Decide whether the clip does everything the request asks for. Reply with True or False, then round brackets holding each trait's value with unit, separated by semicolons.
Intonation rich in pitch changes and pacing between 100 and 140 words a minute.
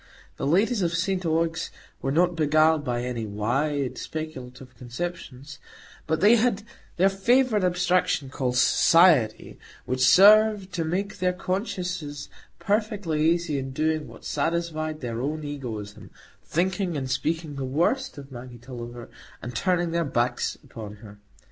True (5.7 semitones; 135 wpm)